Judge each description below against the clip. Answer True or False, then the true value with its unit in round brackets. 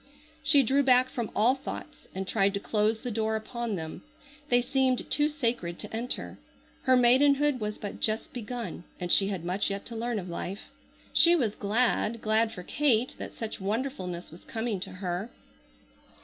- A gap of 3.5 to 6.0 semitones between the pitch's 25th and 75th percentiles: True (4.0 semitones)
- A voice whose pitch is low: False (225 Hz)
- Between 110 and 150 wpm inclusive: False (175 wpm)